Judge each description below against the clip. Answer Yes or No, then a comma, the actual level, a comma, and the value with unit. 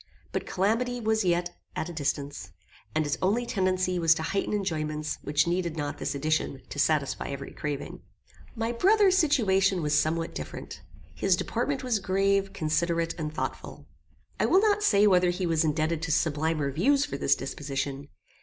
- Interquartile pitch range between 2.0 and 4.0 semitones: No, average, 4.5 semitones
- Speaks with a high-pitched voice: No, medium, 170 Hz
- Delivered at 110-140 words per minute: No, average, 165 wpm